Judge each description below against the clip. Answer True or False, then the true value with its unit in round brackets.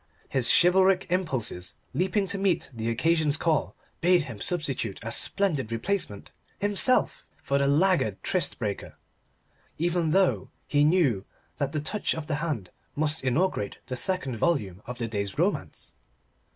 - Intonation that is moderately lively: False (7.5 semitones)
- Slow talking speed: False (145 wpm)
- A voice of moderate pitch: True (150 Hz)